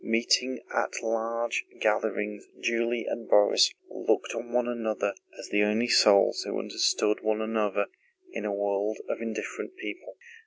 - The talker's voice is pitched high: No, low, 110 Hz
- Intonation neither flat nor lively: No, narrow, 2.0 semitones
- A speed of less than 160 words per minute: Yes, average, 145 wpm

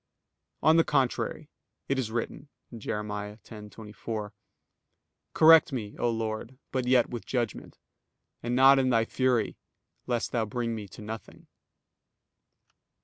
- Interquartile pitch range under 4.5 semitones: Yes, average, 3.1 semitones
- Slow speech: Yes, slow, 125 wpm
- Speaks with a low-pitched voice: Yes, low, 115 Hz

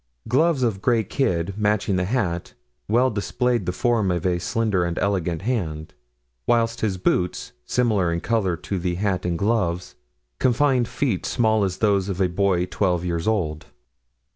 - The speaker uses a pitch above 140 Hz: No, low, 100 Hz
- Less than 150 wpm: No, average, 165 wpm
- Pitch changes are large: No, average, 4.4 semitones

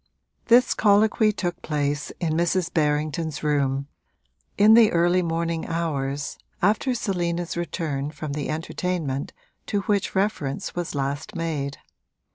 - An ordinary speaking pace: No, slow, 120 wpm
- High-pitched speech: No, medium, 165 Hz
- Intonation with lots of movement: No, average, 4.2 semitones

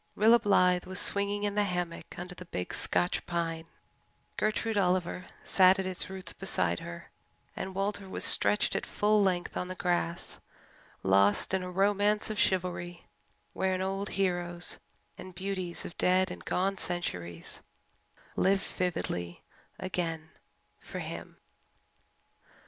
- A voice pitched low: No, medium, 185 Hz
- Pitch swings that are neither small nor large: No, narrow, 2.1 semitones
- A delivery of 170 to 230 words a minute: No, slow, 135 wpm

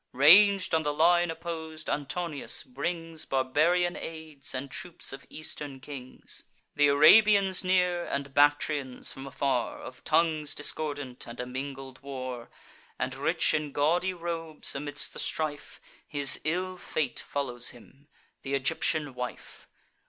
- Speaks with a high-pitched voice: No, medium, 150 Hz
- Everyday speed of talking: No, slow, 130 wpm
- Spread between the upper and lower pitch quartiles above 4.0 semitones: No, average, 3.6 semitones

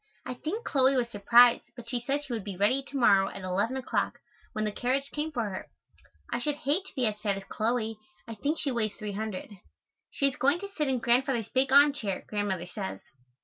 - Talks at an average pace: No, fast, 220 wpm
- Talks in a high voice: Yes, high, 240 Hz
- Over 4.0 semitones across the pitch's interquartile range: Yes, average, 4.7 semitones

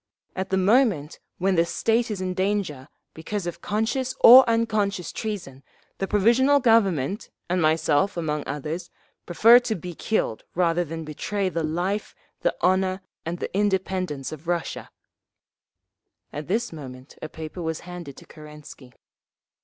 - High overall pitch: No, medium, 180 Hz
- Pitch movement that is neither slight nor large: Yes, average, 4.7 semitones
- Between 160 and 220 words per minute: No, average, 145 wpm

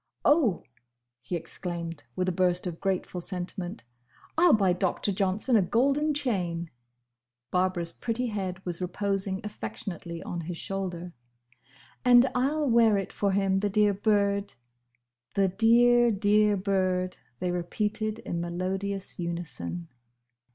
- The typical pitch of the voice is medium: No, high, 195 Hz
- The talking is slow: Yes, slow, 130 wpm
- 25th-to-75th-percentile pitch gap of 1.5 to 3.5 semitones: Yes, average, 3.2 semitones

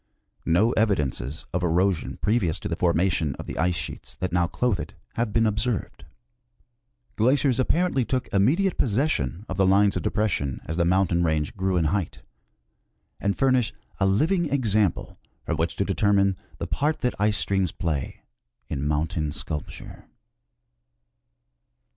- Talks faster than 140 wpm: Yes, average, 150 wpm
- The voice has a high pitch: No, very low, 95 Hz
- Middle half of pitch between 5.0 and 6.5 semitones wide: Yes, average, 5.3 semitones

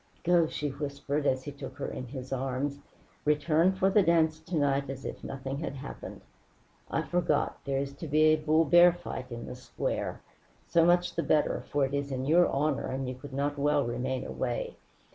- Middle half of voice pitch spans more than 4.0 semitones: No, average, 2.9 semitones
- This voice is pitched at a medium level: Yes, medium, 145 Hz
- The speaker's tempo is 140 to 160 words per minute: No, average, 200 wpm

